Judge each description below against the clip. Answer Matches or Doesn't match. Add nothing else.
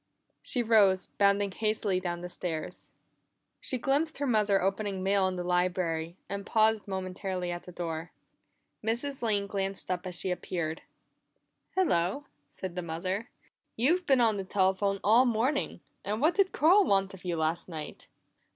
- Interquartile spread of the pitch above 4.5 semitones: Doesn't match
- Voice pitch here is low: Doesn't match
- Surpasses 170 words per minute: Doesn't match